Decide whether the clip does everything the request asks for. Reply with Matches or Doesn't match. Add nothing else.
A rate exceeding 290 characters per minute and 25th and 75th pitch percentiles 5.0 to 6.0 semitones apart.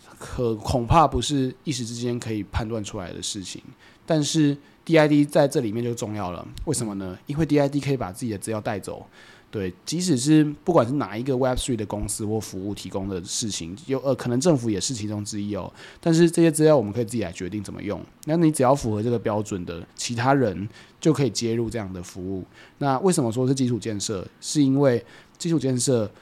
Matches